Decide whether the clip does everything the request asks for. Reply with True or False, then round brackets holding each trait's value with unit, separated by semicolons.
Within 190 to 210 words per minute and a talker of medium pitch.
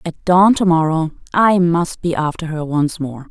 True (200 wpm; 165 Hz)